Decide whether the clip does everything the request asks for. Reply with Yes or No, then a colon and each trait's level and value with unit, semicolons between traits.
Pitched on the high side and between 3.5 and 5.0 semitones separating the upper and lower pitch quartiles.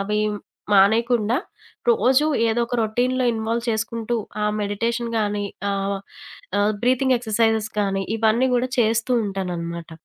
No: high, 220 Hz; average, 2.7 semitones